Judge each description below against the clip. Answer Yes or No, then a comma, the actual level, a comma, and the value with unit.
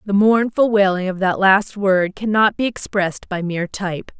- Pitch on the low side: No, high, 195 Hz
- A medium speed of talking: Yes, average, 185 wpm